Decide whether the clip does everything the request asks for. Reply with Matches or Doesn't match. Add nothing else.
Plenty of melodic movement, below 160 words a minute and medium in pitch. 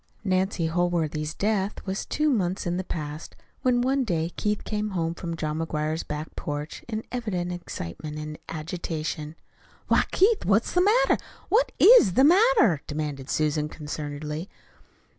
Matches